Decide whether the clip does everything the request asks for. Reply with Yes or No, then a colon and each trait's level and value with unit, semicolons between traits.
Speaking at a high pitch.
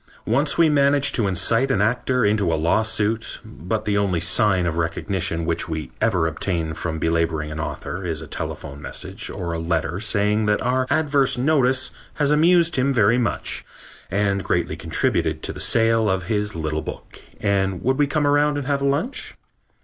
No: low, 105 Hz